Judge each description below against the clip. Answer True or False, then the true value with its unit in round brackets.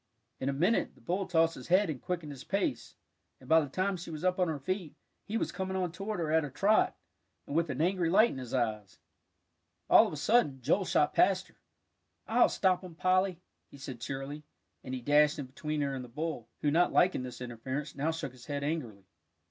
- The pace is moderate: False (225 wpm)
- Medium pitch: True (155 Hz)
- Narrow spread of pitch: False (5.3 semitones)